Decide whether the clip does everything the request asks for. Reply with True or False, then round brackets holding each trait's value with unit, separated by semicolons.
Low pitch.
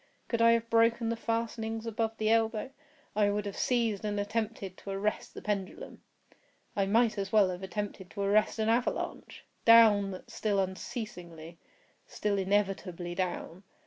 False (210 Hz)